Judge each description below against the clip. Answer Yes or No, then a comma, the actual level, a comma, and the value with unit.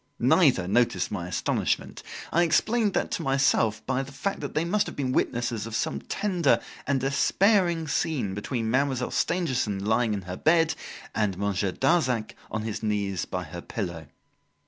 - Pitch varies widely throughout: Yes, wide, 7.5 semitones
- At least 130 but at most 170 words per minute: Yes, average, 165 wpm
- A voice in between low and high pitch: No, low, 125 Hz